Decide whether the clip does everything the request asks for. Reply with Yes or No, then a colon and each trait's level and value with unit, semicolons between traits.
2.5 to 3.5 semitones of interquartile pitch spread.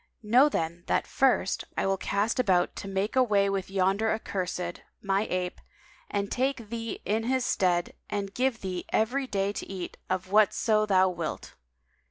Yes: average, 3.1 semitones